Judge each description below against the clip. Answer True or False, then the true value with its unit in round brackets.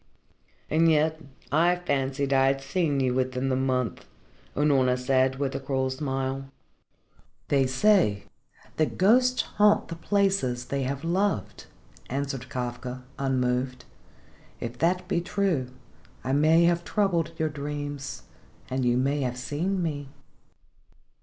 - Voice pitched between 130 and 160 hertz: True (140 Hz)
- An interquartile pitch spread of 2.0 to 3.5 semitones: False (4.2 semitones)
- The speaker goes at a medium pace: False (130 wpm)